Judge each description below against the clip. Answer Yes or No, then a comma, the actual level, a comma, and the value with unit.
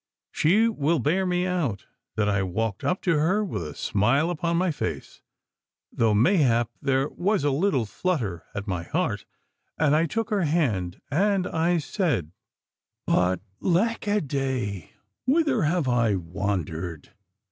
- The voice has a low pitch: No, medium, 145 Hz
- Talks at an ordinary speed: Yes, average, 145 wpm